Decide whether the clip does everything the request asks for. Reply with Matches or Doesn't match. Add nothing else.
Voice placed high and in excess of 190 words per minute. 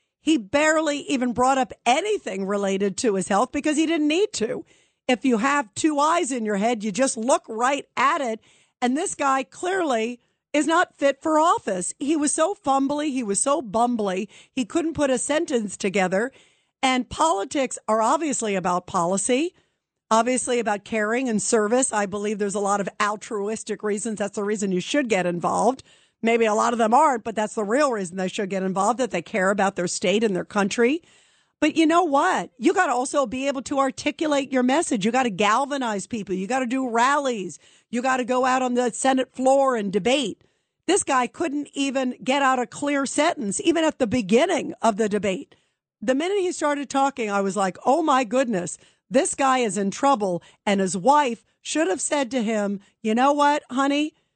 Matches